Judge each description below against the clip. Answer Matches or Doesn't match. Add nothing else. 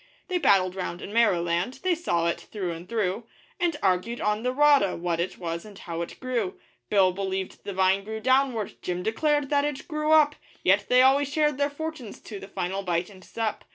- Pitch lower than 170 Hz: Doesn't match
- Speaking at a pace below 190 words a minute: Doesn't match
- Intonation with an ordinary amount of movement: Doesn't match